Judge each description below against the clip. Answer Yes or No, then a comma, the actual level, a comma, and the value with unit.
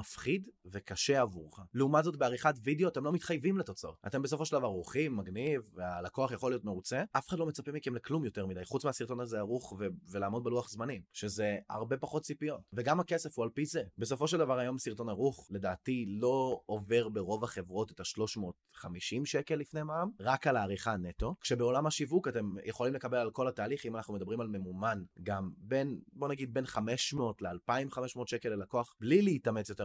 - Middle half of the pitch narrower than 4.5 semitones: No, wide, 5.4 semitones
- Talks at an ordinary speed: No, fast, 175 wpm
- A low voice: Yes, low, 125 Hz